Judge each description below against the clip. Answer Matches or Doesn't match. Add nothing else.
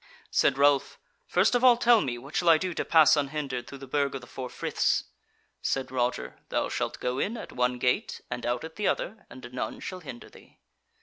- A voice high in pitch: Doesn't match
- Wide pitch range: Doesn't match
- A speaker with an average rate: Doesn't match